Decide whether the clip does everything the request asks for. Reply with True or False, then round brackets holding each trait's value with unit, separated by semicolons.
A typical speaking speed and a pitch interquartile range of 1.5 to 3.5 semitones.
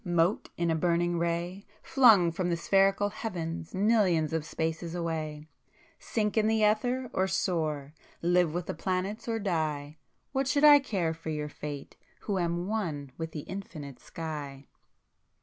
False (155 wpm; 4.0 semitones)